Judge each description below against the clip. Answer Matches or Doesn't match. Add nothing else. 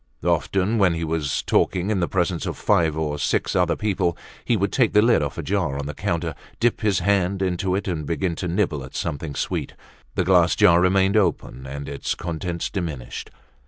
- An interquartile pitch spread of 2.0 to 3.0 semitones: Doesn't match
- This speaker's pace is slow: Doesn't match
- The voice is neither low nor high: Doesn't match